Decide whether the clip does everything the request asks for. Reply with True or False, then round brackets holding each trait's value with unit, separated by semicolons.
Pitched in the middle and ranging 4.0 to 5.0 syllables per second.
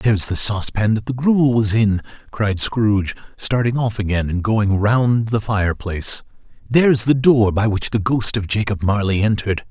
False (110 Hz; 4.9 syllables/s)